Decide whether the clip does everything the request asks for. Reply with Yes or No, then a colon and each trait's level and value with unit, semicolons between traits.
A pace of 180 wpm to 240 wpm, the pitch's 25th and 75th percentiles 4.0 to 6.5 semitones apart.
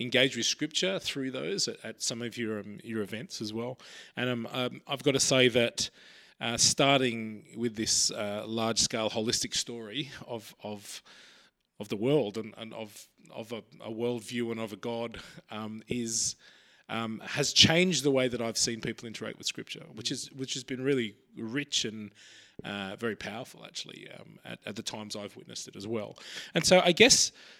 No: average, 185 wpm; average, 3.0 semitones